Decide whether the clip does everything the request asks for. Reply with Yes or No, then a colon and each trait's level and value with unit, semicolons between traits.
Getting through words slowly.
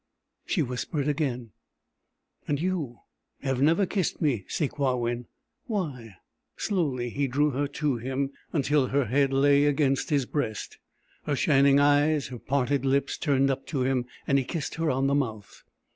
No: average, 155 wpm